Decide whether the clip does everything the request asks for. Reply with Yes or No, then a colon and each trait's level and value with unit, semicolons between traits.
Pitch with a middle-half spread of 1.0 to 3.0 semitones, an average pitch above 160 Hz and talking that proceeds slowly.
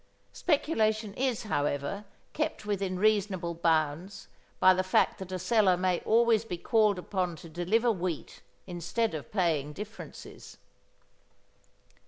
No: average, 3.9 semitones; high, 190 Hz; slow, 125 wpm